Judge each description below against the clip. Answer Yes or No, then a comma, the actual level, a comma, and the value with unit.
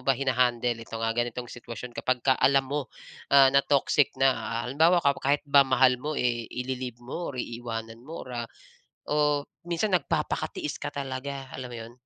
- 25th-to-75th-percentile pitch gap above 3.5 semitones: No, narrow, 2.6 semitones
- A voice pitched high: No, low, 130 Hz